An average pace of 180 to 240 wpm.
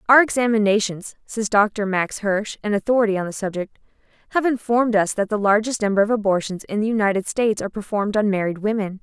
Yes: average, 195 wpm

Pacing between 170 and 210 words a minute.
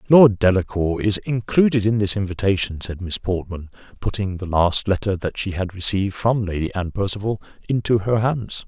Yes: average, 175 wpm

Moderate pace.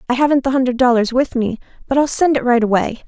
No: fast, 255 wpm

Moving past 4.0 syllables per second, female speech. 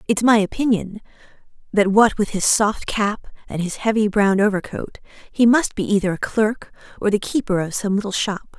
Yes: 5.0 syllables/s; female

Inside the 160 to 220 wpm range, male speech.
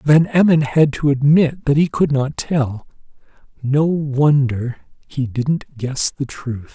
No: average, 150 wpm; male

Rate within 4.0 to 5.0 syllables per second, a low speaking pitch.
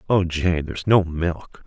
Yes: 4.1 syllables/s; very low, 85 Hz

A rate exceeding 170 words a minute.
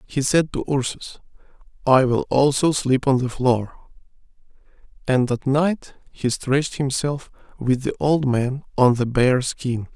No: average, 150 wpm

